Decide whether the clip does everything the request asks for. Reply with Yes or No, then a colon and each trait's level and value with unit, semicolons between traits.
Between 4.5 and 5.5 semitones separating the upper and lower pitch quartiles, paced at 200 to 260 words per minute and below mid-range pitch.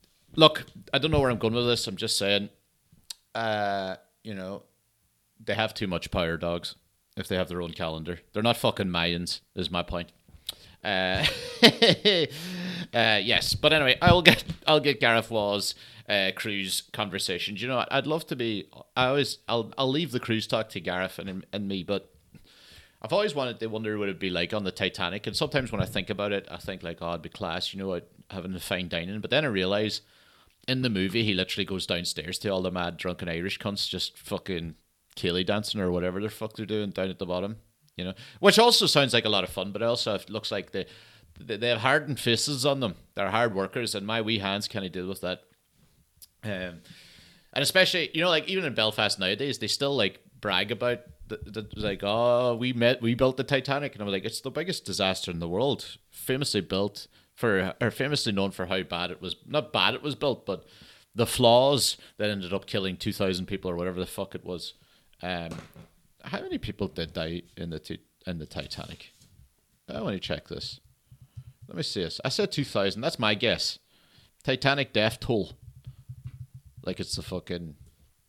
Yes: average, 4.8 semitones; fast, 205 wpm; low, 105 Hz